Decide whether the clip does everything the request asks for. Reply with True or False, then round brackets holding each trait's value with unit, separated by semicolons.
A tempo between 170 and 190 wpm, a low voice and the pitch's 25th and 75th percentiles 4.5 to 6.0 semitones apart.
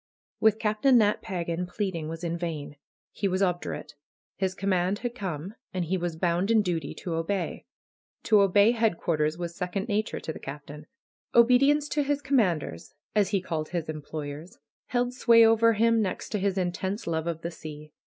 False (180 wpm; 185 Hz; 4.8 semitones)